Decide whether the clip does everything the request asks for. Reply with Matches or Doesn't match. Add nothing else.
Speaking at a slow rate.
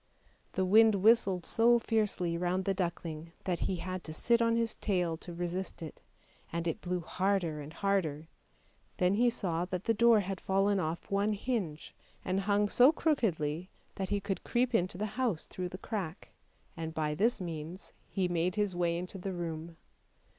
Doesn't match